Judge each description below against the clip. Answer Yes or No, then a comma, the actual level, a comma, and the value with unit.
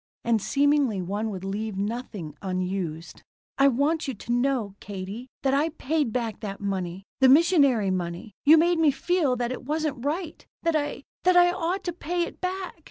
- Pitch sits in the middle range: No, very high, 255 Hz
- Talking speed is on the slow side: No, average, 180 wpm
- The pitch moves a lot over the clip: Yes, wide, 7.8 semitones